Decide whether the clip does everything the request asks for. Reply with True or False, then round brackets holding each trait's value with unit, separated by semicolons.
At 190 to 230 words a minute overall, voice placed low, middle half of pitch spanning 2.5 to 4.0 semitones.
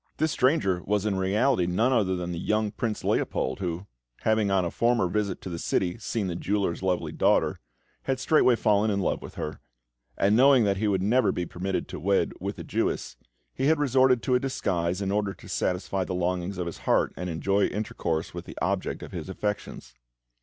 True (205 wpm; 100 Hz; 3.7 semitones)